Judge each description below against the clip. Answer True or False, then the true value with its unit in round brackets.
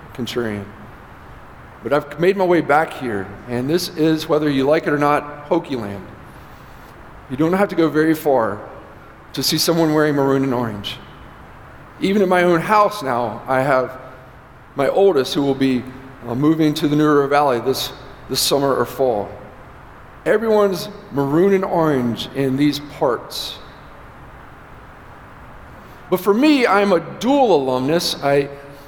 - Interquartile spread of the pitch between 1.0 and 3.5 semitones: False (4.2 semitones)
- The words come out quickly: False (150 wpm)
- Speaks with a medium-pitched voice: True (145 Hz)